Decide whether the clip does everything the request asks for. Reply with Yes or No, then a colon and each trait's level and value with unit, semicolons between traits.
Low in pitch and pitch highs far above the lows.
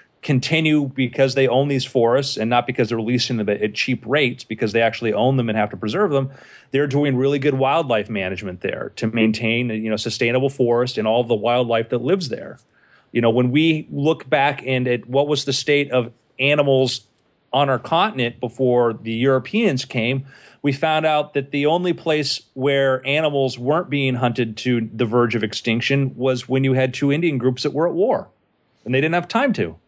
No: low, 130 Hz; average, 3.1 semitones